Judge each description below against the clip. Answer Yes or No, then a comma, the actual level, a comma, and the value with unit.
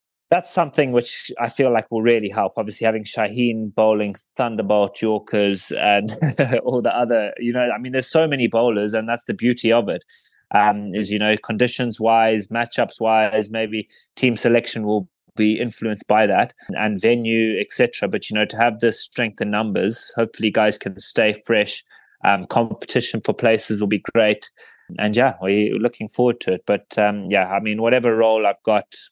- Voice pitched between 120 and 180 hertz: No, low, 110 Hz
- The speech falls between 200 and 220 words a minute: No, average, 185 wpm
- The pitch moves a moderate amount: No, narrow, 2.1 semitones